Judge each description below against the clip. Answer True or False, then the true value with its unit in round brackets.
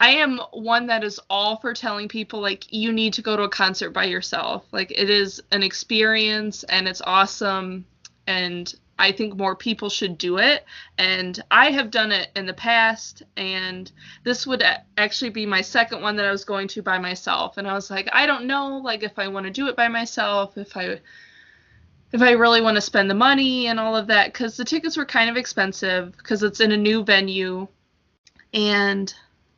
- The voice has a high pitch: True (210 Hz)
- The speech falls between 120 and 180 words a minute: False (205 wpm)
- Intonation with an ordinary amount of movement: True (3.1 semitones)